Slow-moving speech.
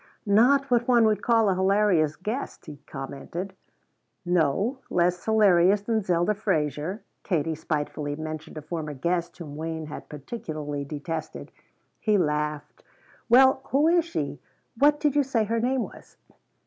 No: average, 145 wpm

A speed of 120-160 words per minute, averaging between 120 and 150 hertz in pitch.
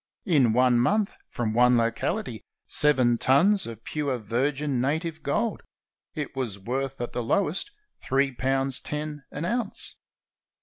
Yes: slow, 135 wpm; low, 135 Hz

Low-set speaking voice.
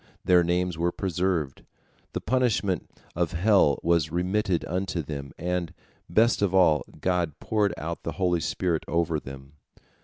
Yes: very low, 90 Hz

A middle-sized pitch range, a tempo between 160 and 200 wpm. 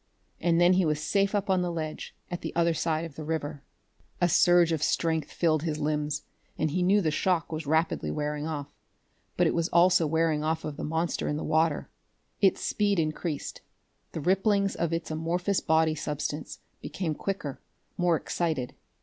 No: narrow, 2.3 semitones; average, 185 wpm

